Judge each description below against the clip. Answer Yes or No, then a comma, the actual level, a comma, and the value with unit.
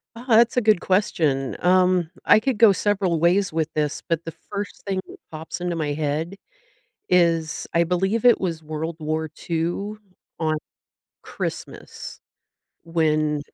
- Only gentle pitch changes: No, average, 3.8 semitones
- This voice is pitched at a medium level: Yes, medium, 170 Hz